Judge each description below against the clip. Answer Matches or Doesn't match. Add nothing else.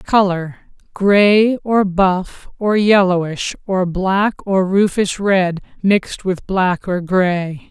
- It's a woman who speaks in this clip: Matches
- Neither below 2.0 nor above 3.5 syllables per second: Matches